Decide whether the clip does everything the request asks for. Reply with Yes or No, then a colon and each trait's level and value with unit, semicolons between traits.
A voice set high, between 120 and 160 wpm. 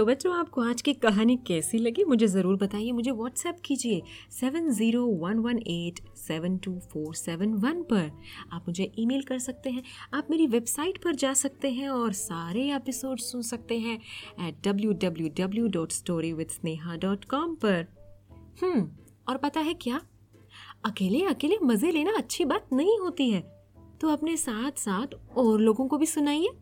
Yes: high, 230 Hz; average, 150 wpm